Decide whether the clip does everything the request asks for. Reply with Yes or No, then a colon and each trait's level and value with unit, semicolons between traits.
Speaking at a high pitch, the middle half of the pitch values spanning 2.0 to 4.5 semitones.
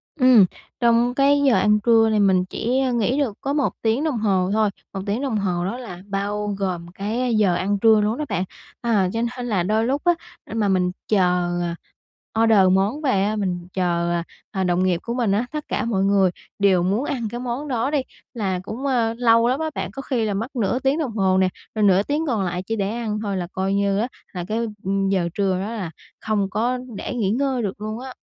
Yes: high, 215 Hz; average, 4.0 semitones